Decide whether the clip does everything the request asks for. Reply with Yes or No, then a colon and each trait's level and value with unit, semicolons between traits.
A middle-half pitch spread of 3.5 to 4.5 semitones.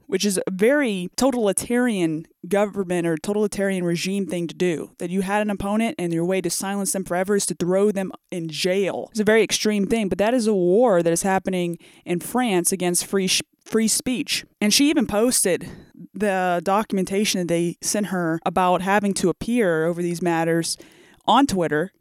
No: average, 3.0 semitones